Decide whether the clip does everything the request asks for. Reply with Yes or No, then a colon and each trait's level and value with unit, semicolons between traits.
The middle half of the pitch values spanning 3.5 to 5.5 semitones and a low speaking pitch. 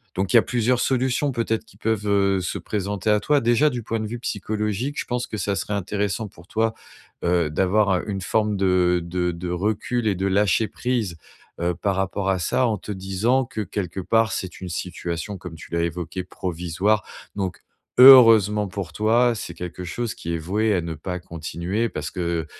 Yes: average, 3.8 semitones; low, 100 Hz